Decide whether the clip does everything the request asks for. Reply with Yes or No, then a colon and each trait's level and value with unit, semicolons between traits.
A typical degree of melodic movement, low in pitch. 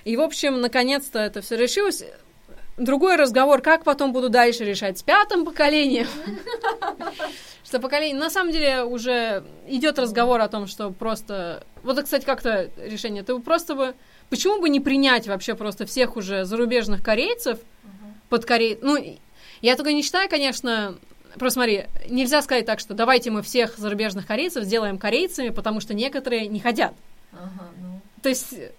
No: average, 4.8 semitones; very high, 250 Hz